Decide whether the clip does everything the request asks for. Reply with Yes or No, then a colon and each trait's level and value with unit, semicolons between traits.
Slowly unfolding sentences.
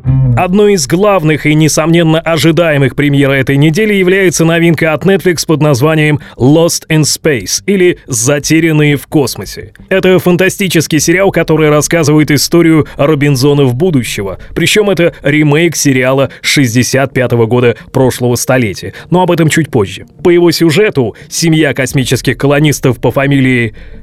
No: average, 125 wpm